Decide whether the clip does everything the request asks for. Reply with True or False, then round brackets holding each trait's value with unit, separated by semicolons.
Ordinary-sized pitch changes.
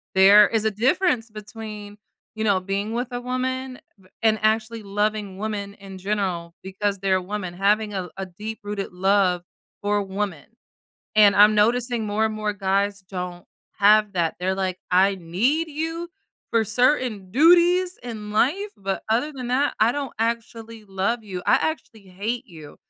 True (3.2 semitones)